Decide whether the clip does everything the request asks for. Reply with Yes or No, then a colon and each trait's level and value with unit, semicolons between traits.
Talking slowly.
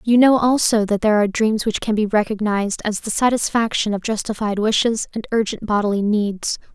No: average, 185 wpm